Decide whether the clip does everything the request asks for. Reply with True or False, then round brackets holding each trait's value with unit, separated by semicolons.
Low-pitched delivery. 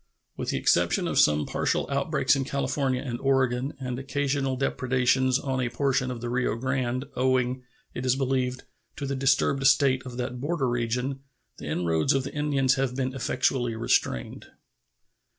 True (130 Hz)